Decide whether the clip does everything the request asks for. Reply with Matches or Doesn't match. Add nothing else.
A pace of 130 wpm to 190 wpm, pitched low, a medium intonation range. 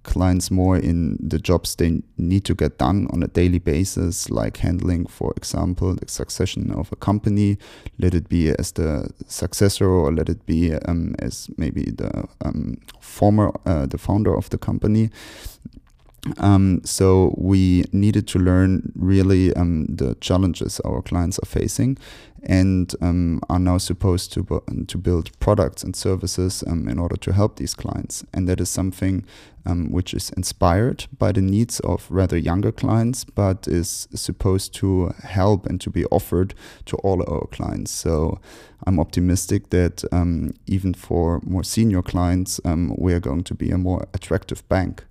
Doesn't match